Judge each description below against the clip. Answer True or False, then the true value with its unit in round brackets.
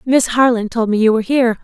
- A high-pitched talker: True (235 Hz)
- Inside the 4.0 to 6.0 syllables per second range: False (6.7 syllables/s)